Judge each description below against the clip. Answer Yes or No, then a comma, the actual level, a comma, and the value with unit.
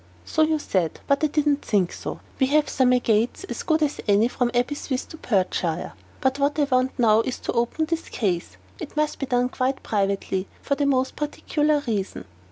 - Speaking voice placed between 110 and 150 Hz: No, very high, 255 Hz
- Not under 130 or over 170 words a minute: No, average, 200 wpm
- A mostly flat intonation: No, wide, 5.4 semitones